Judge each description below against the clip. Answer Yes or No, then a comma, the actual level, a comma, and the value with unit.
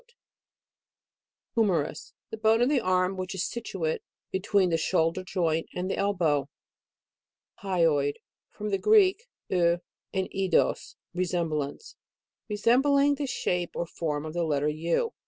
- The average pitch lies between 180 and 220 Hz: Yes, medium, 185 Hz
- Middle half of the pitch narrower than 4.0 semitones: No, average, 4.7 semitones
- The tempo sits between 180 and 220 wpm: No, slow, 135 wpm